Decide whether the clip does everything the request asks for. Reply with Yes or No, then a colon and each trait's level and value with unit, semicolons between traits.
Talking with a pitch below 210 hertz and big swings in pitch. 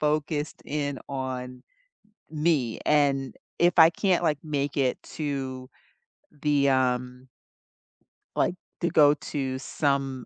No: medium, 140 Hz; narrow, 2.5 semitones